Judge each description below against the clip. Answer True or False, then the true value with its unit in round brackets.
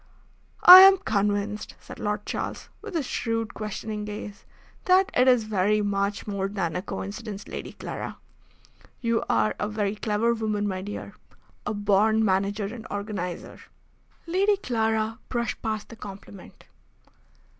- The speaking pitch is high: True (210 Hz)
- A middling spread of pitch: False (2.1 semitones)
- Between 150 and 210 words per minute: False (140 wpm)